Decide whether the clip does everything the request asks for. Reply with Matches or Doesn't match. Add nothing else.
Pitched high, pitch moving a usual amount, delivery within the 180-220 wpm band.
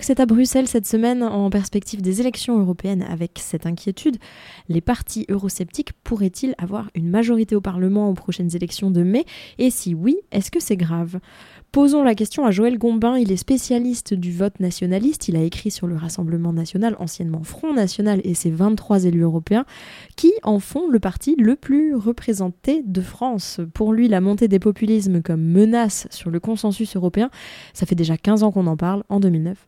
Matches